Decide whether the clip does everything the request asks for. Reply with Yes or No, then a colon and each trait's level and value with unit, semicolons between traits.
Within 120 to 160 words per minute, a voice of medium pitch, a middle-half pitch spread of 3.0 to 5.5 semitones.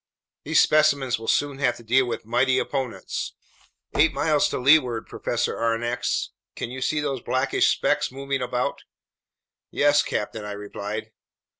No: average, 145 wpm; low, 130 Hz; average, 3.4 semitones